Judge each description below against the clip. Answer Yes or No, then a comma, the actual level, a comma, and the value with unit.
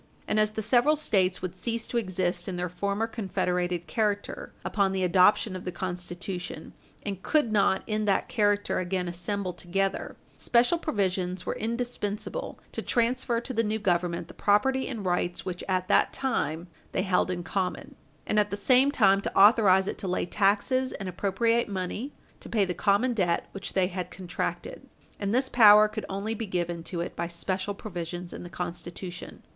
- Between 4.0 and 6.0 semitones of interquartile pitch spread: No, average, 3.3 semitones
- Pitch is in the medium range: No, high, 195 Hz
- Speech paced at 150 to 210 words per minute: Yes, average, 180 wpm